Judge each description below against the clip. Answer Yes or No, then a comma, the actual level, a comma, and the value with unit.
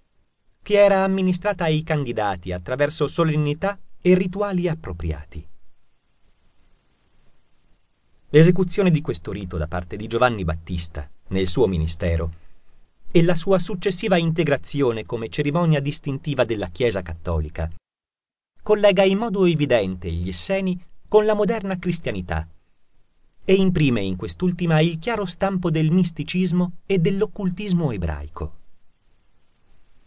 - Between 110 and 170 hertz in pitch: Yes, medium, 140 Hz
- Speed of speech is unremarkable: No, slow, 110 wpm